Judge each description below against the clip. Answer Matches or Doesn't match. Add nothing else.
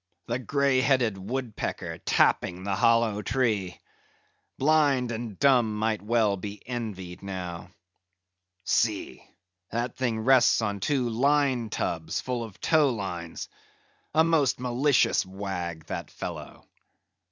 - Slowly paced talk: Matches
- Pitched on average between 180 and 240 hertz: Doesn't match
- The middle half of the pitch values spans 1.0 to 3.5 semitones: Doesn't match